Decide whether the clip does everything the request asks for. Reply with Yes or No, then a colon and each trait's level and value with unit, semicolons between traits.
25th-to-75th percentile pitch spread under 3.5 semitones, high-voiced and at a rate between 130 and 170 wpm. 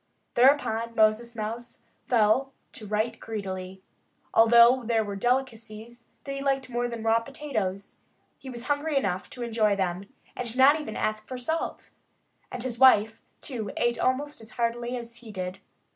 Yes: average, 2.9 semitones; high, 235 Hz; average, 160 wpm